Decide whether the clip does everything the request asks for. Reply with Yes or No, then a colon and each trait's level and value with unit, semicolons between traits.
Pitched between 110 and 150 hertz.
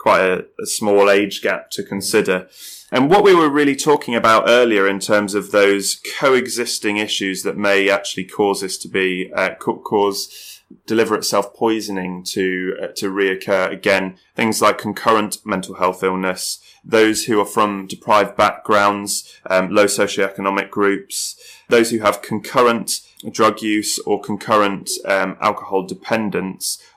No: low, 100 Hz